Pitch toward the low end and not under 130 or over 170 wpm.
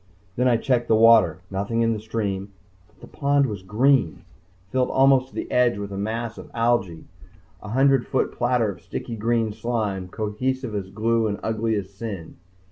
No: low, 115 Hz; average, 185 wpm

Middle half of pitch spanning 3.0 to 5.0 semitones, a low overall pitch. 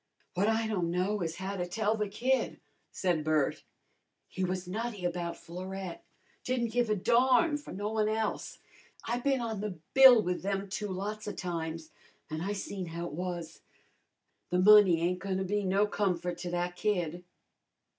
No: average, 3.3 semitones; high, 195 Hz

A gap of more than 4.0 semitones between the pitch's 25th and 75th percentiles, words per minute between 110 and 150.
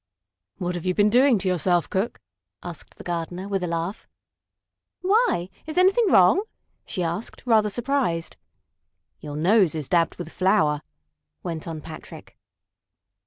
Yes: average, 5.0 semitones; average, 140 wpm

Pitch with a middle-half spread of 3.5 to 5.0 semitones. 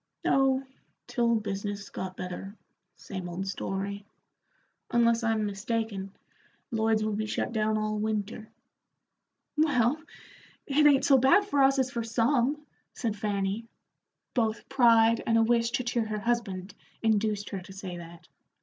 No: average, 3.0 semitones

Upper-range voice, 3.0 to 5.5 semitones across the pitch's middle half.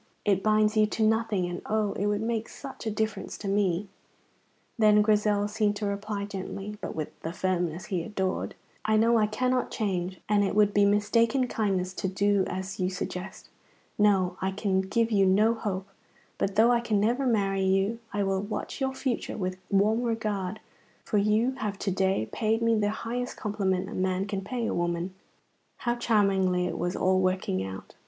No: high, 205 Hz; narrow, 2.4 semitones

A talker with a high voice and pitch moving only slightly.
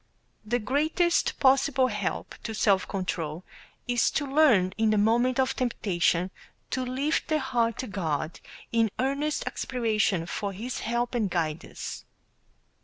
No: high, 230 Hz; average, 5.1 semitones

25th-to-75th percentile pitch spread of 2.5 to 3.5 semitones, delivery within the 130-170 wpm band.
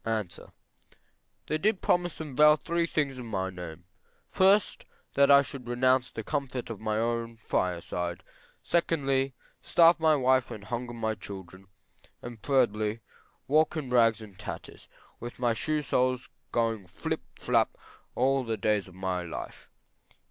No: average, 4.7 semitones; average, 150 wpm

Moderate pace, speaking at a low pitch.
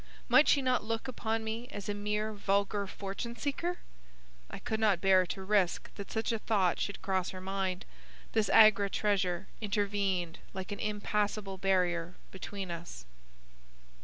No: average, 155 wpm; high, 200 Hz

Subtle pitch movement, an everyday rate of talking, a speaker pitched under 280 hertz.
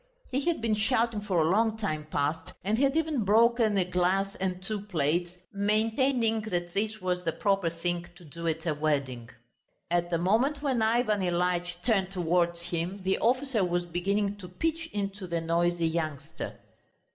No: average, 4.2 semitones; average, 170 wpm; high, 190 Hz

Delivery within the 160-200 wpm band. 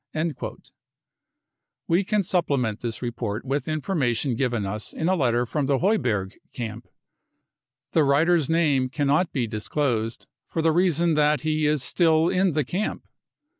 No: average, 150 wpm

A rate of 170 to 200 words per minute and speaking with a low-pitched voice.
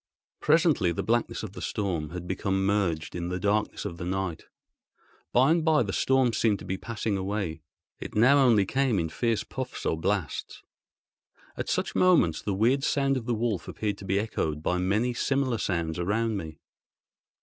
Yes: average, 185 wpm; low, 105 Hz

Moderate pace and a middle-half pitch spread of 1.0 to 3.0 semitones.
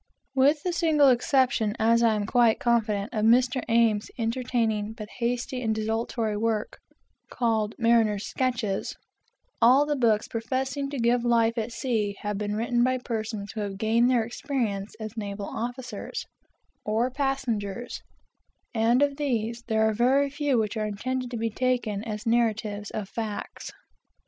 Yes: average, 155 wpm; average, 2.7 semitones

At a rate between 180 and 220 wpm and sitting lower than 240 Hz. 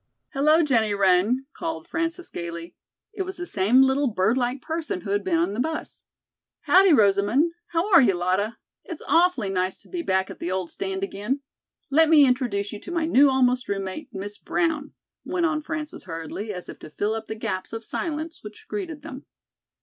No: average, 195 wpm; very high, 250 Hz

